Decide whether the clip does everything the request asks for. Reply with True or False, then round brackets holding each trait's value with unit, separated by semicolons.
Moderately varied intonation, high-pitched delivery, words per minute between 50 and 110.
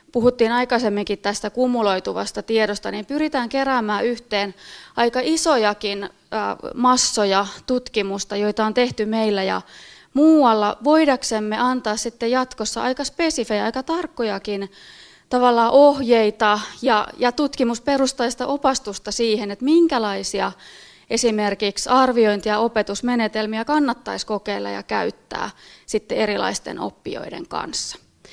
True (3.4 semitones; 230 Hz; 100 wpm)